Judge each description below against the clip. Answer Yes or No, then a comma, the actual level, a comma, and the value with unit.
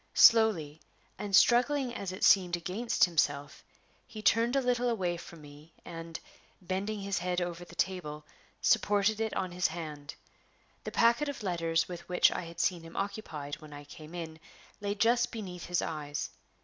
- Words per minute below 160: No, average, 170 wpm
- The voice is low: No, medium, 180 Hz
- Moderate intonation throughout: Yes, average, 4.7 semitones